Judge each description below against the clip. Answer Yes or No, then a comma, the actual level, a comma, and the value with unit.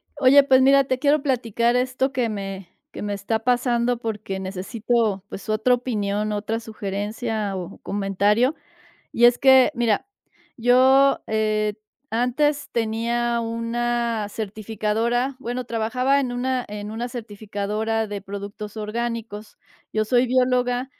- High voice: Yes, high, 230 Hz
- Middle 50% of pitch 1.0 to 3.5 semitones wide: Yes, average, 2.9 semitones